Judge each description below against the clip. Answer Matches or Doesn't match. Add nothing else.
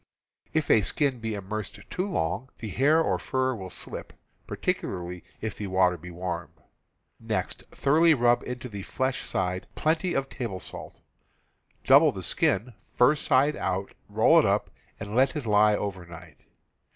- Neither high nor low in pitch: Doesn't match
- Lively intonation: Matches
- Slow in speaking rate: Doesn't match